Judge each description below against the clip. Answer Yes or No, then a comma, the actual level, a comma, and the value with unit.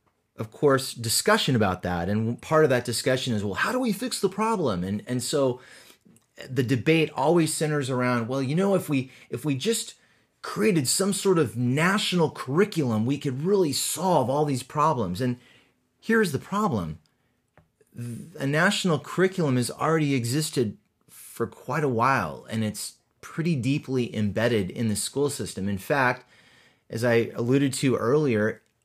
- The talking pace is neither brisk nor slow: Yes, average, 160 wpm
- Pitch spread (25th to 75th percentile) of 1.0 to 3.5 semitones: No, wide, 5.6 semitones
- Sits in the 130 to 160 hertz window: Yes, low, 135 Hz